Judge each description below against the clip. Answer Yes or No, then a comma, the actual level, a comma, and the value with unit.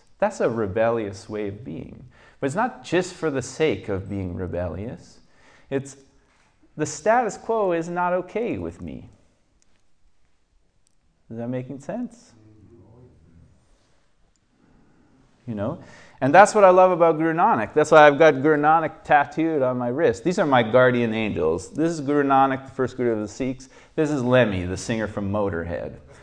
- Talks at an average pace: Yes, average, 160 wpm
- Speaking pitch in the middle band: No, low, 125 Hz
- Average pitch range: No, wide, 7.0 semitones